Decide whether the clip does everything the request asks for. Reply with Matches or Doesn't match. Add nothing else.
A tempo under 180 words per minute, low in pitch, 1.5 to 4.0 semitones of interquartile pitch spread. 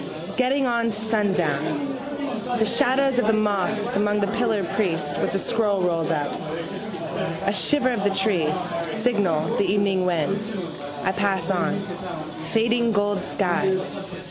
Doesn't match